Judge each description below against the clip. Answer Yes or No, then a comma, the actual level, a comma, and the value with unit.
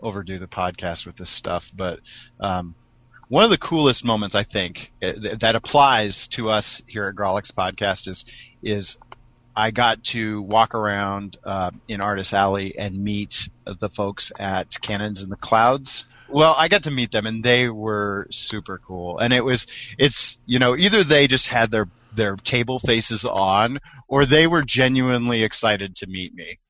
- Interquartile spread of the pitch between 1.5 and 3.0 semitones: No, average, 3.8 semitones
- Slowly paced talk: No, average, 175 wpm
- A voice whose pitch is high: No, low, 110 Hz